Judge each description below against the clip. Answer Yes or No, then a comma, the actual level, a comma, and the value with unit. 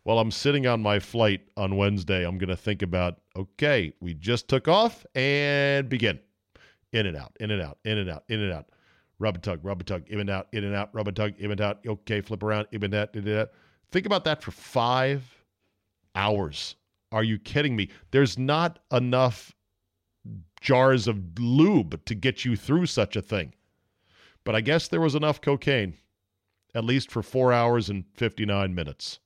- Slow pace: No, average, 200 wpm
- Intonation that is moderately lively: Yes, average, 4.7 semitones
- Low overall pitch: Yes, low, 105 Hz